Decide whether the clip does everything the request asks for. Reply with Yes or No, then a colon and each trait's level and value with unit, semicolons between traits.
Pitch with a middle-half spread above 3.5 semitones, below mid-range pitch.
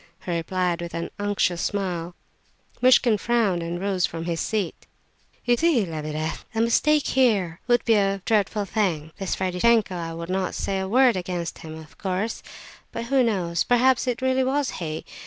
No: wide, 5.4 semitones; high, 195 Hz